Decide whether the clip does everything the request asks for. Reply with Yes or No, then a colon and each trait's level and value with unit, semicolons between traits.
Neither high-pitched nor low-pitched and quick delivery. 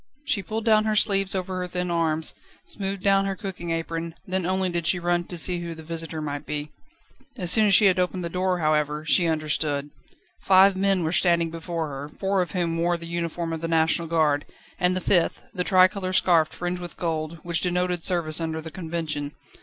Yes: medium, 175 Hz; fast, 210 wpm